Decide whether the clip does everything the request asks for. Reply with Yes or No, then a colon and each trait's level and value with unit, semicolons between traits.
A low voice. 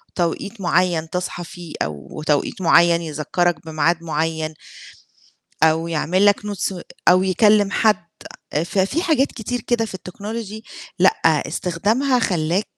No: medium, 180 Hz